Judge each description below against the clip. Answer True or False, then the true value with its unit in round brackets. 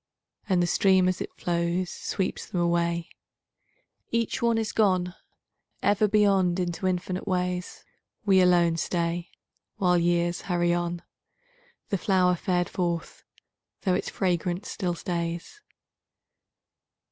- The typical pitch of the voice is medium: True (180 Hz)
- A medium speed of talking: False (120 wpm)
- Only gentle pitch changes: True (1.5 semitones)